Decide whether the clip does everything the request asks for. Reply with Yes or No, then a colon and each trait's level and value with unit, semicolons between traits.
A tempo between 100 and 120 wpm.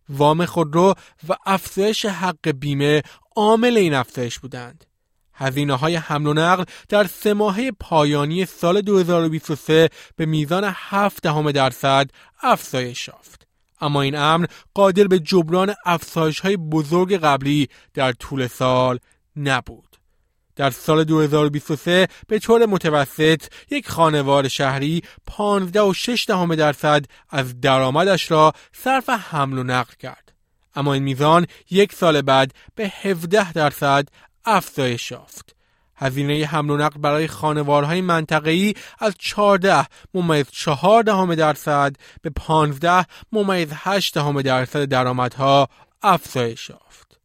Yes: average, 115 wpm